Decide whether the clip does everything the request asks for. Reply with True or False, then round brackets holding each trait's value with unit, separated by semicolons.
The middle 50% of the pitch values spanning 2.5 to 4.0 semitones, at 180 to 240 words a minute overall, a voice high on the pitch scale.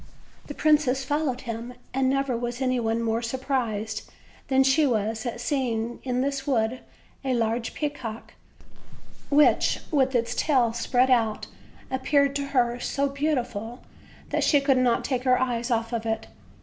False (2.8 semitones; 150 wpm; 250 Hz)